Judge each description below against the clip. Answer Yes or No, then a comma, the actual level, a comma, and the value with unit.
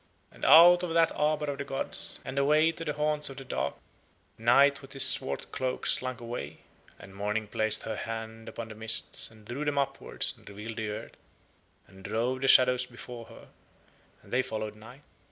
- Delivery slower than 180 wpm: No, average, 190 wpm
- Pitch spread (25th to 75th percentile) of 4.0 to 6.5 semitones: Yes, average, 4.3 semitones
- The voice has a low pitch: Yes, low, 125 Hz